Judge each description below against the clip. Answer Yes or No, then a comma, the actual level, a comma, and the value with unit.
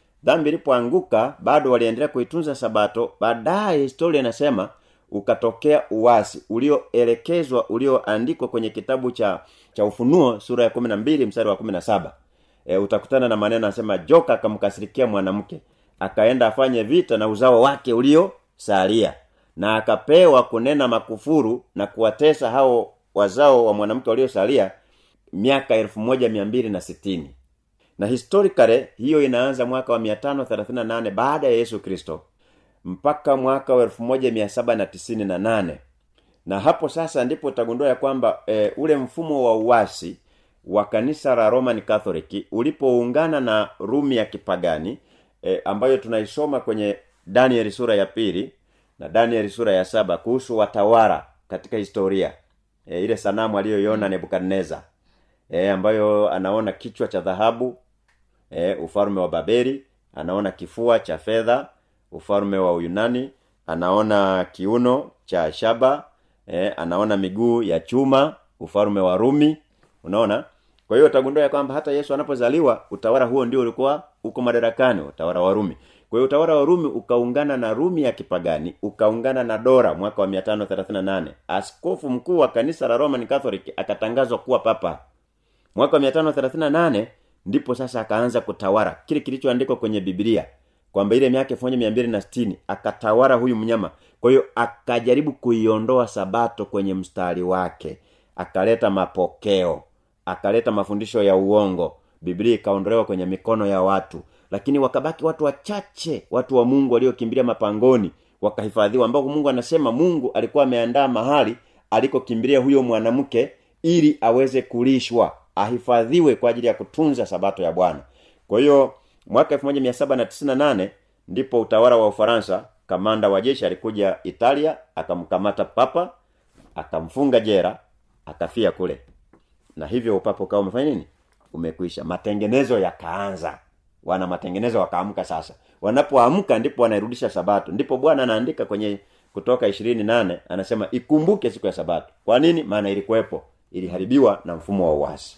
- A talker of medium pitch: No, low, 115 Hz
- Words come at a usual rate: Yes, average, 110 wpm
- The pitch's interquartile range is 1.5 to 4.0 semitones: No, average, 4.7 semitones